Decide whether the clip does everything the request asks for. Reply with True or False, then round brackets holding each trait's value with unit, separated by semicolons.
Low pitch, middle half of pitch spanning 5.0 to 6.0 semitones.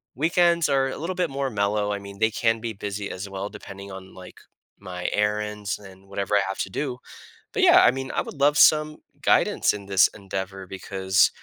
True (105 Hz; 5.3 semitones)